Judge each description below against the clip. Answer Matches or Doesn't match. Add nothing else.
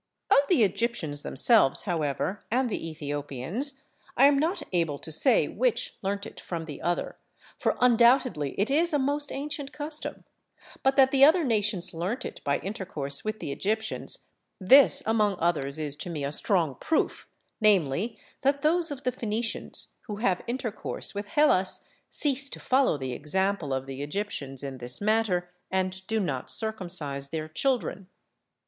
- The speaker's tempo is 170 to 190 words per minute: Doesn't match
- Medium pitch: Doesn't match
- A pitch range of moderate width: Doesn't match